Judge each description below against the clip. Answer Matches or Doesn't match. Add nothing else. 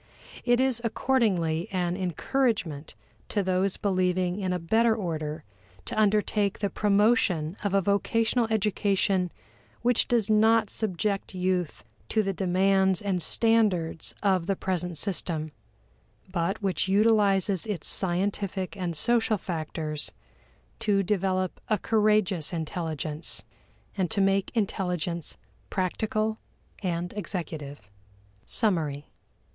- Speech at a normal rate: Doesn't match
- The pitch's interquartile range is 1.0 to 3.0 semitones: Doesn't match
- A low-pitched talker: Doesn't match